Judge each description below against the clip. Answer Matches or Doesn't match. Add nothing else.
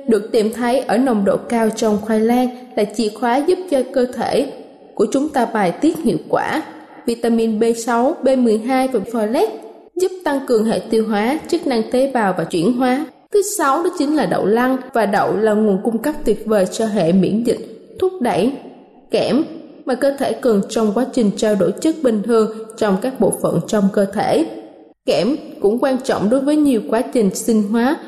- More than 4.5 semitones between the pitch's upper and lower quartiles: Doesn't match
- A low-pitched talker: Doesn't match